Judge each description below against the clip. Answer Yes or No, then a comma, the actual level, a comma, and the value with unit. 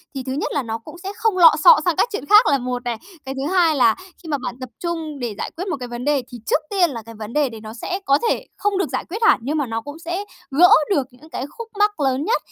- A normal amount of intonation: No, wide, 6.1 semitones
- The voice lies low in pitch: No, very high, 290 Hz